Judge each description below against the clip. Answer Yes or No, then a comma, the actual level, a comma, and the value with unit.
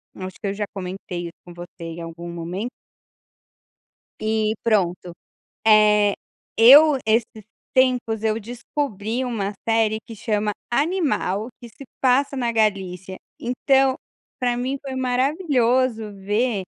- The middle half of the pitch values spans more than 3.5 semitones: Yes, average, 4.3 semitones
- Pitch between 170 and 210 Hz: No, high, 220 Hz